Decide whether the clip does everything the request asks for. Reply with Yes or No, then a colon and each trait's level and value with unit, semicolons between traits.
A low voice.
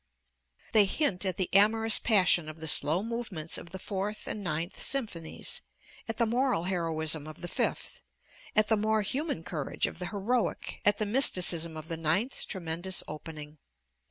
No: high, 190 Hz